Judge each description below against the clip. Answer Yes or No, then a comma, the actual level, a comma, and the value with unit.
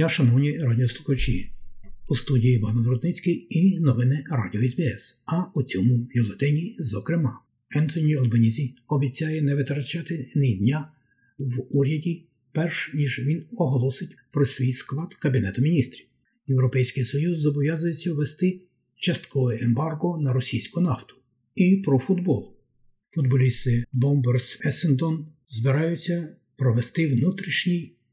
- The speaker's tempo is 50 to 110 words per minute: Yes, slow, 105 wpm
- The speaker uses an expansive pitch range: No, average, 4.5 semitones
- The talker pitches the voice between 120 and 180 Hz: Yes, medium, 140 Hz